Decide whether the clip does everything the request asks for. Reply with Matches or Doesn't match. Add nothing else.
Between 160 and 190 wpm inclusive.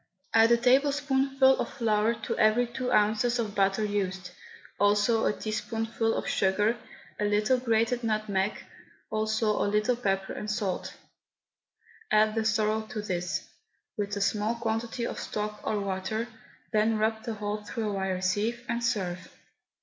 Doesn't match